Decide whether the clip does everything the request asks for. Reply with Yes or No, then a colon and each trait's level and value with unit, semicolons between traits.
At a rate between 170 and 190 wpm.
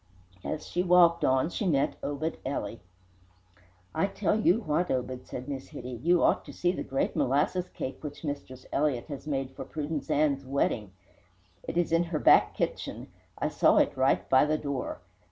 Yes: average, 180 wpm